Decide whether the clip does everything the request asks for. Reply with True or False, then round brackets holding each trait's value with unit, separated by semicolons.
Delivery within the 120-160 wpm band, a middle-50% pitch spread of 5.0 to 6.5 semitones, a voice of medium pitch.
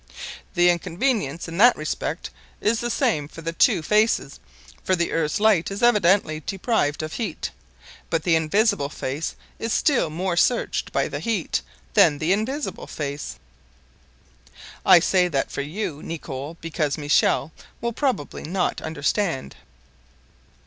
True (140 wpm; 5.5 semitones; 170 Hz)